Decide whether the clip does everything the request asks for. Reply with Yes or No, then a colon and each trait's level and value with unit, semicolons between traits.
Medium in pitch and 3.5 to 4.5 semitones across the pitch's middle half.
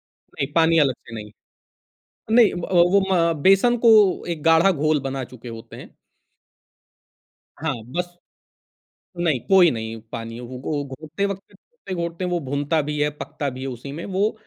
No: medium, 155 Hz; average, 4.9 semitones